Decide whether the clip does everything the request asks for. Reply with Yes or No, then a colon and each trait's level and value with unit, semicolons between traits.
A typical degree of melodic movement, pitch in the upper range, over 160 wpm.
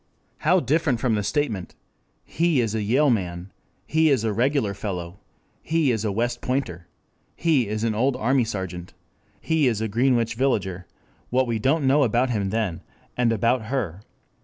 No: average, 4.8 semitones; low, 115 Hz; average, 170 wpm